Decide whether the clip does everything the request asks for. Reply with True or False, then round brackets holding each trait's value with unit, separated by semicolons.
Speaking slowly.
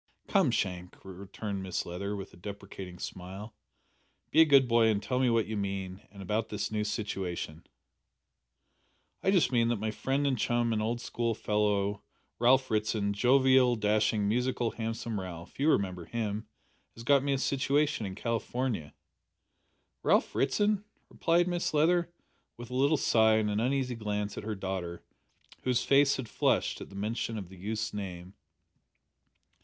False (160 wpm)